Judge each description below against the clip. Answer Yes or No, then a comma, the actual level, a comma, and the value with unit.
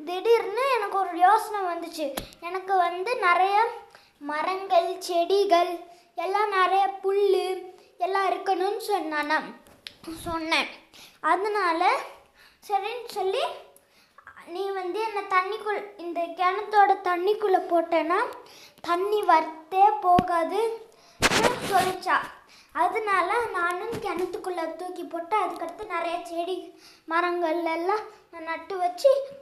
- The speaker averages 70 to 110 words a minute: Yes, average, 95 wpm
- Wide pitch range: No, average, 2.9 semitones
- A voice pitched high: Yes, very high, 365 Hz